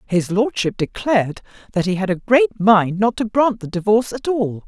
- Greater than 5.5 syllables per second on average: No, 5.0 syllables/s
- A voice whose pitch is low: No, high, 210 Hz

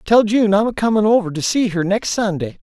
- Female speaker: No, male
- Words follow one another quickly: Yes, fast, 245 wpm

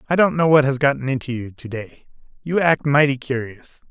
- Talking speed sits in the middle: No, fast, 215 wpm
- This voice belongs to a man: Yes, male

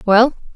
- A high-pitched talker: Yes, high, 230 Hz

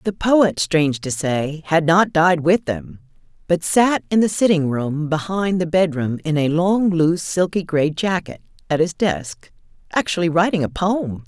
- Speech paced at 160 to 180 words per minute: Yes, average, 170 wpm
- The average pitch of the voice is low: No, medium, 170 Hz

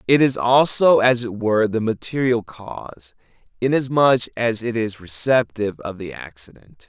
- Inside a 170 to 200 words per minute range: No, average, 150 wpm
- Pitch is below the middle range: Yes, low, 115 Hz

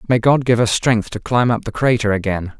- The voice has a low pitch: Yes, low, 115 Hz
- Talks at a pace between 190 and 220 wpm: No, fast, 255 wpm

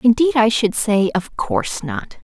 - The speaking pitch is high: Yes, high, 225 Hz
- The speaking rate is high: No, average, 180 wpm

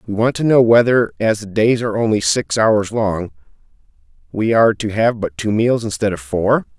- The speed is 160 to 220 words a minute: Yes, fast, 205 wpm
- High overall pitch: No, low, 105 Hz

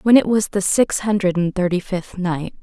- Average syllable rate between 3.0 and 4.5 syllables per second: No, 4.8 syllables/s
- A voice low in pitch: No, high, 190 Hz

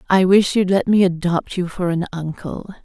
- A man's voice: No, female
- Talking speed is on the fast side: Yes, fast, 210 wpm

